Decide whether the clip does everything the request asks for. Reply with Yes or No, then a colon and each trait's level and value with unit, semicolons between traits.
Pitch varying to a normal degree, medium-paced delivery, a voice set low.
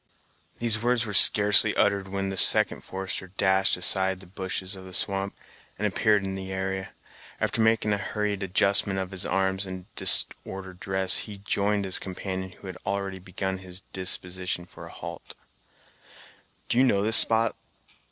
No: narrow, 1.3 semitones; average, 165 wpm; very low, 95 Hz